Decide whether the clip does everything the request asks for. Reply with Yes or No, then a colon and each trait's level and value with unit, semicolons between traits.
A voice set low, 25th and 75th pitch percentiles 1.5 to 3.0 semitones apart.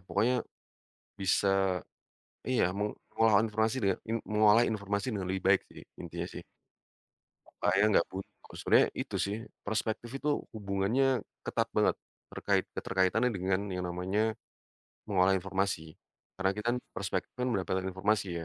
Yes: low, 100 Hz; average, 2.7 semitones